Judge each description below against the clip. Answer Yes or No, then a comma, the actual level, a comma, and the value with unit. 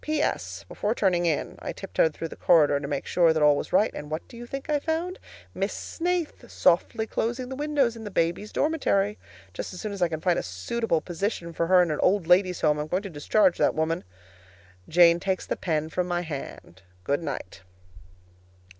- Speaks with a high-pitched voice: No, medium, 180 Hz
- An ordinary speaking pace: No, fast, 210 wpm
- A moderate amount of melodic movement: No, wide, 5.8 semitones